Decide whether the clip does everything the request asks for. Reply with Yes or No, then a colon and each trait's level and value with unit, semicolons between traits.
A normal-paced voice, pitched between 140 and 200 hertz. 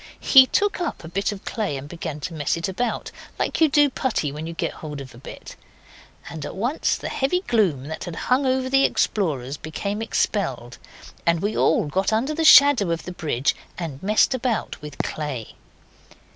Yes: average, 195 wpm; medium, 185 Hz